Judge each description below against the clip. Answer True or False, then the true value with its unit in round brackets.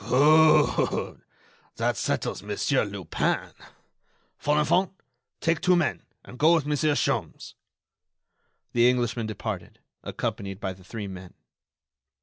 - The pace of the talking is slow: True (110 wpm)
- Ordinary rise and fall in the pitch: False (6.1 semitones)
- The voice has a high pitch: False (125 Hz)